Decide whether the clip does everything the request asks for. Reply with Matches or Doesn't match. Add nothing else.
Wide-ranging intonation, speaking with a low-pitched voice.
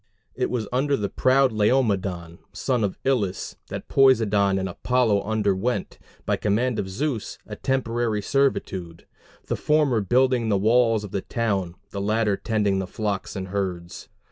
Doesn't match